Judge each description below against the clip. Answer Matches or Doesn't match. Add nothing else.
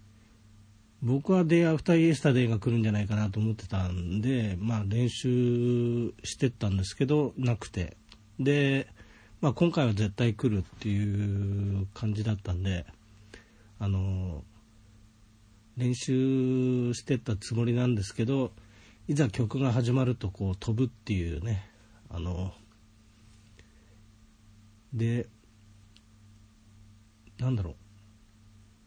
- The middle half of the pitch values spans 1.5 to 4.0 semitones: Matches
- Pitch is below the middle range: Matches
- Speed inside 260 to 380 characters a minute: Doesn't match